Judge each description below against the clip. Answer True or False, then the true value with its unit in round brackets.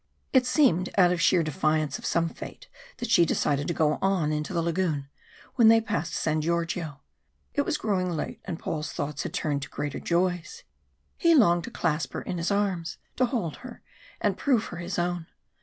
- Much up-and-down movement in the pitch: False (4.3 semitones)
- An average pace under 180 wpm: False (195 wpm)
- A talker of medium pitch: True (170 Hz)